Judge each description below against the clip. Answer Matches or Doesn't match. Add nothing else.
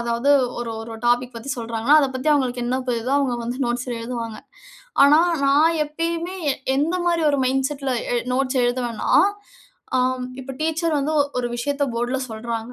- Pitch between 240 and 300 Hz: Matches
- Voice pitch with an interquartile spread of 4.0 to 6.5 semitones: Doesn't match